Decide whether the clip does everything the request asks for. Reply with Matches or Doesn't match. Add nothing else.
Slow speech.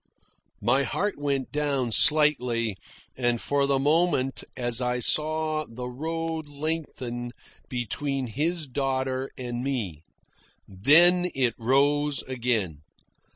Matches